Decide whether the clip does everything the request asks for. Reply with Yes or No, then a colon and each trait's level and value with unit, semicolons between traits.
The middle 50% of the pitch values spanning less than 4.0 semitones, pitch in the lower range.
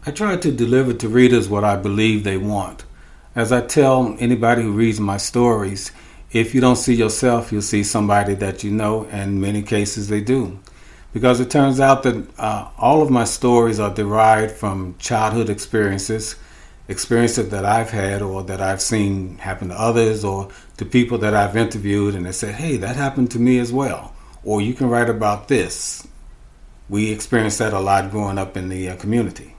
Yes: average, 3.0 semitones; low, 110 Hz